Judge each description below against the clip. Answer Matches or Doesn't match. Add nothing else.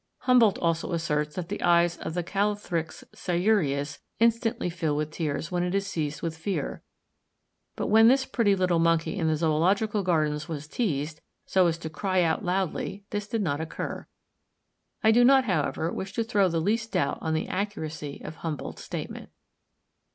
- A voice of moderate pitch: Matches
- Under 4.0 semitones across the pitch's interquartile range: Doesn't match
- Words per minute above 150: Matches